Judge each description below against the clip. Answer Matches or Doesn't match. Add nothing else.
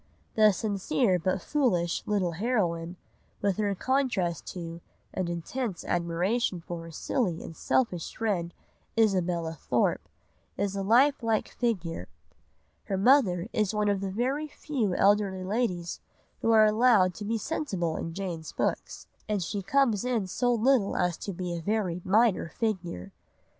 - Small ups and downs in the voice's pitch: Doesn't match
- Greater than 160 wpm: Doesn't match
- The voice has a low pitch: Doesn't match